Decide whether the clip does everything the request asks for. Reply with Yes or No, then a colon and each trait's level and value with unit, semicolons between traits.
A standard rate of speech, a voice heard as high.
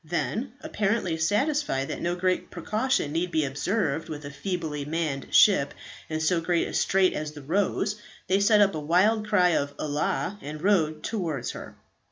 No: average, 175 wpm; medium, 170 Hz